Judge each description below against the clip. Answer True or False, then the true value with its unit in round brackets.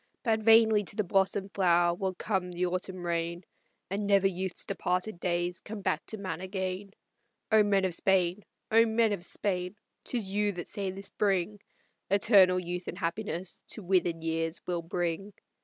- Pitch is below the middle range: False (190 Hz)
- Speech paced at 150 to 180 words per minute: True (170 wpm)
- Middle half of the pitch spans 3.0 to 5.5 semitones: False (2.6 semitones)